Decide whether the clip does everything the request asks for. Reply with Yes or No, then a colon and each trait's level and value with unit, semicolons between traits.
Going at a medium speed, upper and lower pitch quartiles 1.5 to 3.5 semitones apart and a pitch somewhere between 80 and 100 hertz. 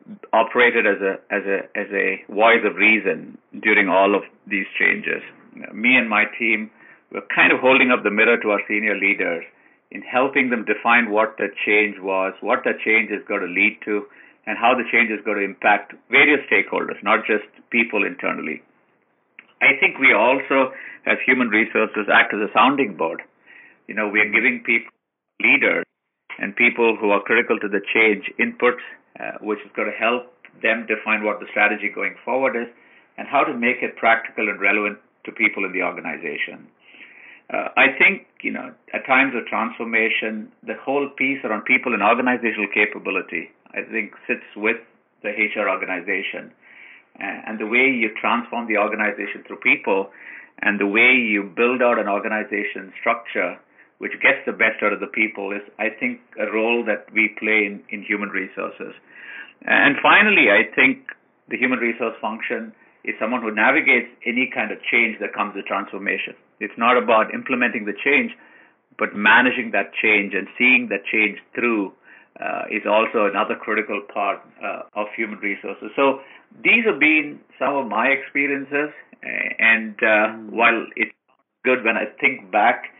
No: average, 175 wpm; average, 2.8 semitones; low, 110 Hz